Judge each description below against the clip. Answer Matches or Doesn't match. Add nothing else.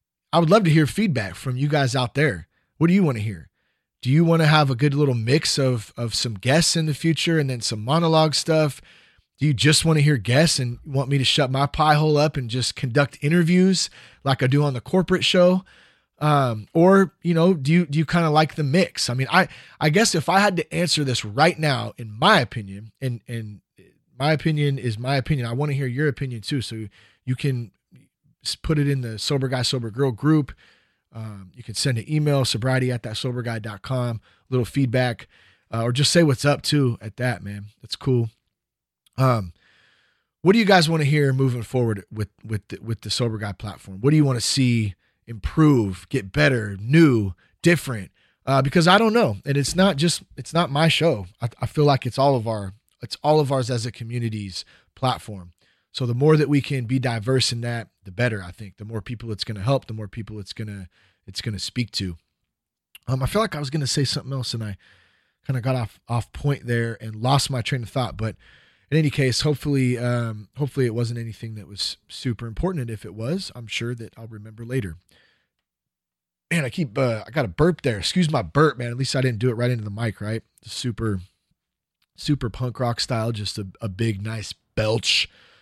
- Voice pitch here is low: Matches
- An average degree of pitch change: Matches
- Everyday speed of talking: Doesn't match